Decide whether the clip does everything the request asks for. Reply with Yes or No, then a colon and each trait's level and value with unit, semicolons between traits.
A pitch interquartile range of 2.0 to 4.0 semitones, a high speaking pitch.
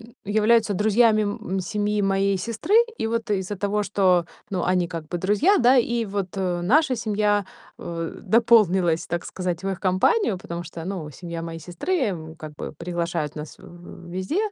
Yes: average, 3.7 semitones; high, 195 Hz